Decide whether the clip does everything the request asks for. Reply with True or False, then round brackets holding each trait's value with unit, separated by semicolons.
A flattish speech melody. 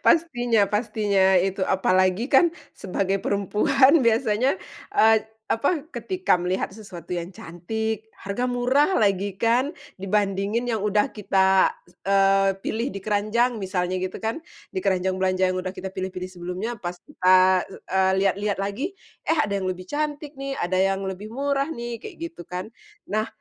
False (4.1 semitones)